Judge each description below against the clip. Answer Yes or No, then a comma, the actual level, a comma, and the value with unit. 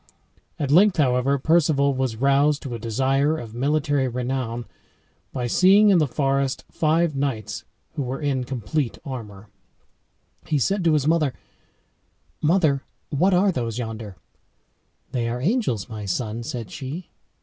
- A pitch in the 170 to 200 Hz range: No, low, 135 Hz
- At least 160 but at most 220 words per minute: No, average, 140 wpm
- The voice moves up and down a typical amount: Yes, average, 4.3 semitones